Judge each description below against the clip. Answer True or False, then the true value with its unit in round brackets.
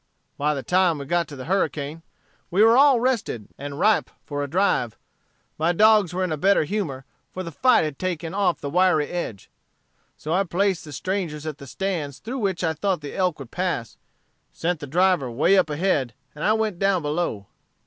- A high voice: False (175 Hz)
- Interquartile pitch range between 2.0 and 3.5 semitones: False (4.7 semitones)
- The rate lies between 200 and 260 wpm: True (205 wpm)